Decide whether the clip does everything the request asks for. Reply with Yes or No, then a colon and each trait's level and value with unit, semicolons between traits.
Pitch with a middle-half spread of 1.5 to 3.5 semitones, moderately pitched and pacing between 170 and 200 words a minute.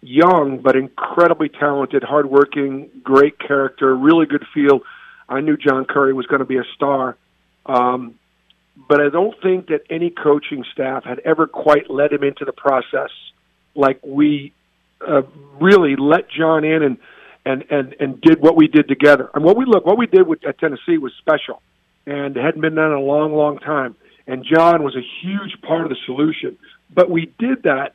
Yes: average, 2.8 semitones; medium, 145 Hz; average, 190 wpm